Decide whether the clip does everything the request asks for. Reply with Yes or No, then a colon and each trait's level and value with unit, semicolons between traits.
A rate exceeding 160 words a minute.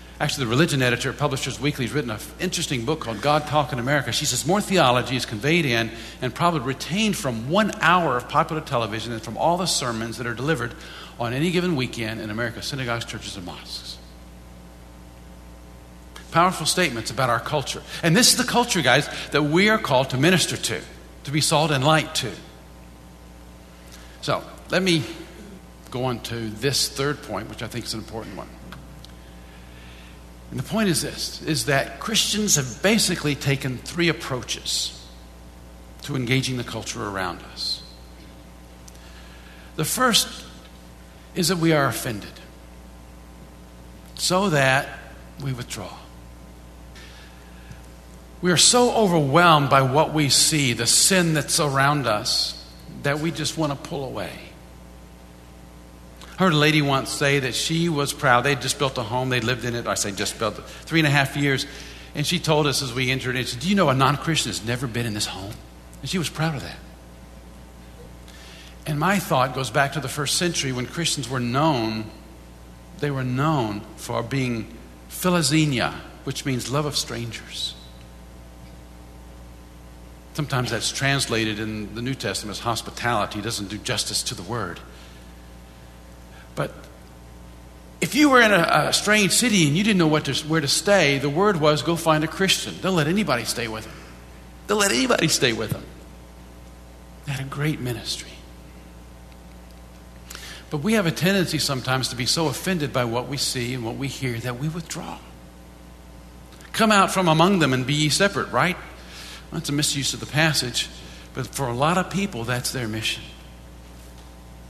Yes: average, 170 wpm